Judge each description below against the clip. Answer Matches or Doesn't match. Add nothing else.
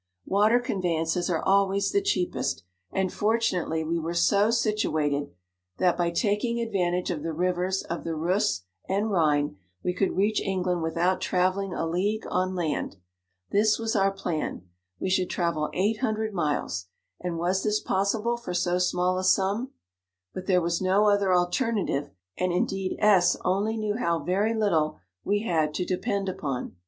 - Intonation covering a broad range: Doesn't match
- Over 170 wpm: Doesn't match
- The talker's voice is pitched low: Doesn't match